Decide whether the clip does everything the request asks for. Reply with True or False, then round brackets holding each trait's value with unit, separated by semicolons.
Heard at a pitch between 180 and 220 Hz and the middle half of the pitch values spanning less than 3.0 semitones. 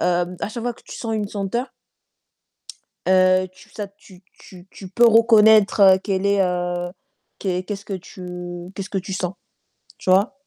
True (190 Hz; 2.4 semitones)